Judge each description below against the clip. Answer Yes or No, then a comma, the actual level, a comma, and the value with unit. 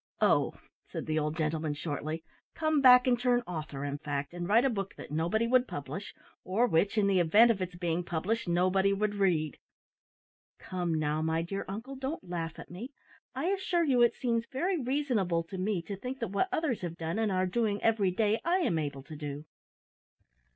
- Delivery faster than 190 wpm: Yes, average, 200 wpm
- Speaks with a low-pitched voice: No, high, 195 Hz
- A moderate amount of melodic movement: No, wide, 6.6 semitones